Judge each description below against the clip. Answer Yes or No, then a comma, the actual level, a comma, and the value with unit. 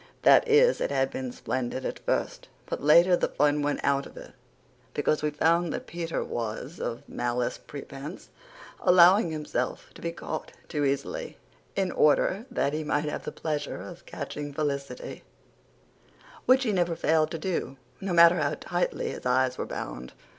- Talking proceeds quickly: No, average, 170 wpm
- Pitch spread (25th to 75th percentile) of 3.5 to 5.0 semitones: Yes, average, 4.0 semitones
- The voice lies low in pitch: No, medium, 150 Hz